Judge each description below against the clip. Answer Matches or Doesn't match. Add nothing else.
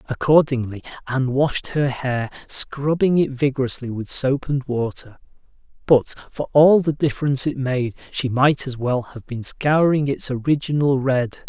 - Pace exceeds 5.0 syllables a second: Doesn't match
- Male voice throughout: Matches